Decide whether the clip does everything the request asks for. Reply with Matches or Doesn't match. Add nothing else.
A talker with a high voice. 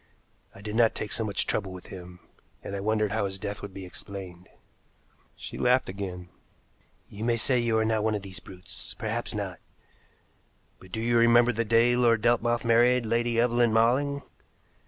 Doesn't match